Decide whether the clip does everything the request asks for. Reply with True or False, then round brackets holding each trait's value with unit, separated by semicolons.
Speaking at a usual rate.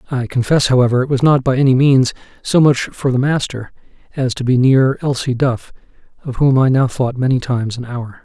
False (210 wpm)